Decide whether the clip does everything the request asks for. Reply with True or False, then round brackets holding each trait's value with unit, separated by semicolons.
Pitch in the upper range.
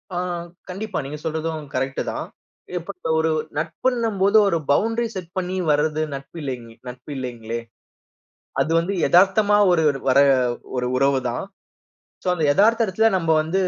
False (165 Hz)